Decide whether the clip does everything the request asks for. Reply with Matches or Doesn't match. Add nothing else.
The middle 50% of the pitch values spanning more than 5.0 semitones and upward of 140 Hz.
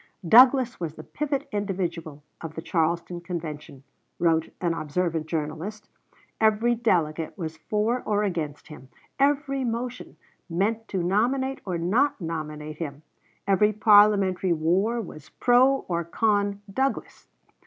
Matches